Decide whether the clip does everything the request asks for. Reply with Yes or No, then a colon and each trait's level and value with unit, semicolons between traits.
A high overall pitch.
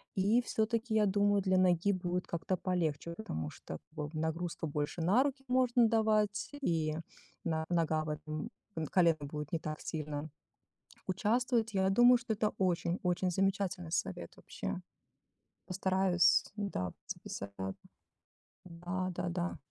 No: medium, 180 Hz